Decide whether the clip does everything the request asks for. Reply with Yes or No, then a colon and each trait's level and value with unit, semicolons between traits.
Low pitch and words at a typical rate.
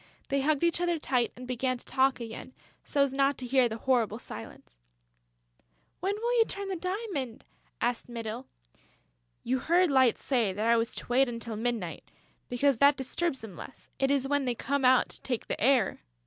No: very high, 260 Hz; average, 190 wpm